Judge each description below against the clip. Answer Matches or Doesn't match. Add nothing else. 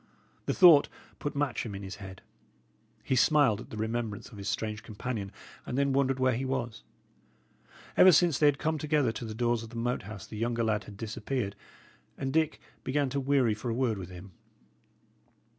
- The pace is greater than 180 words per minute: Matches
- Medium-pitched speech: Doesn't match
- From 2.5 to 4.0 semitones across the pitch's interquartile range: Doesn't match